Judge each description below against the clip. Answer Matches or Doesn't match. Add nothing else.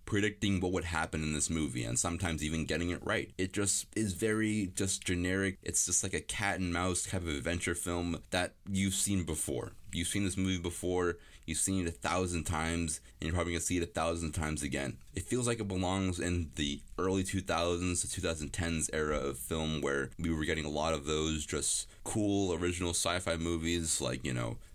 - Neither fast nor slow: Doesn't match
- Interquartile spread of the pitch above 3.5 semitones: Doesn't match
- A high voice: Doesn't match